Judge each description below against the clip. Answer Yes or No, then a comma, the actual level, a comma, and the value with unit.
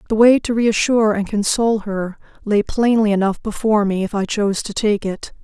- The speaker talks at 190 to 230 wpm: Yes, average, 200 wpm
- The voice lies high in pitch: Yes, high, 210 Hz